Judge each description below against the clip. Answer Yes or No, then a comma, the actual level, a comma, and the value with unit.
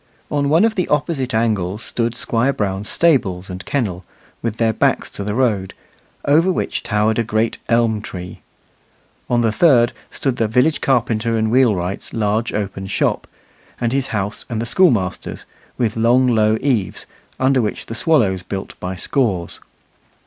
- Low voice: Yes, low, 115 Hz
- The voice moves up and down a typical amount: Yes, average, 3.9 semitones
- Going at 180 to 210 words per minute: No, average, 160 wpm